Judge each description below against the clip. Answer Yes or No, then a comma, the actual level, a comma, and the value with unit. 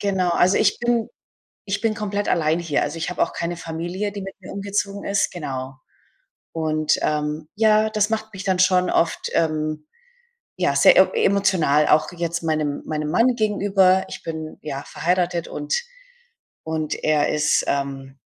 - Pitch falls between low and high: Yes, medium, 175 Hz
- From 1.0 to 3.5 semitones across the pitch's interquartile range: No, average, 4.6 semitones